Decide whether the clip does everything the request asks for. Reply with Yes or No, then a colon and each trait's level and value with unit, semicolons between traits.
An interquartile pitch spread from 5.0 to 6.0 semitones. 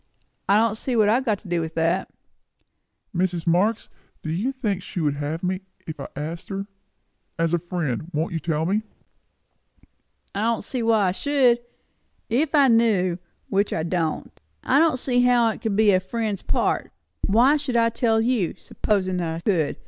Yes: wide, 5.4 semitones